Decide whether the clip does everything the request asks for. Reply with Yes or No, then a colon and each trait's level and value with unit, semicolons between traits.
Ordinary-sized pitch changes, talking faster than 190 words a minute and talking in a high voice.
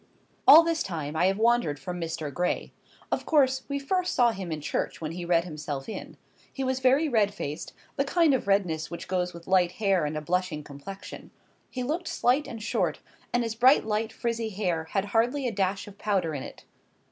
No: wide, 6.5 semitones; fast, 205 wpm; high, 195 Hz